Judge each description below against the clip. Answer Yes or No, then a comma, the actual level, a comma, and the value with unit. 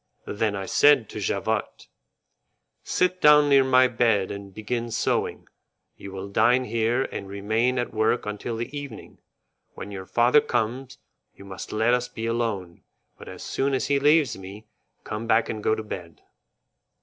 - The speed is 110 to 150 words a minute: No, average, 165 wpm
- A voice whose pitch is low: Yes, low, 115 Hz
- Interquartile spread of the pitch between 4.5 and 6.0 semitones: No, average, 3.9 semitones